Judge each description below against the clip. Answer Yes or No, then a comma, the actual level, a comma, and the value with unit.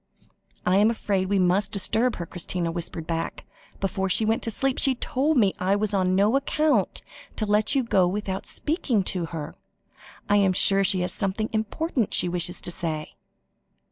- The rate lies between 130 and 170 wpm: No, average, 180 wpm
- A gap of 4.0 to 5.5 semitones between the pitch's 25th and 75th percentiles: No, average, 3.4 semitones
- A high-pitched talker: Yes, high, 195 Hz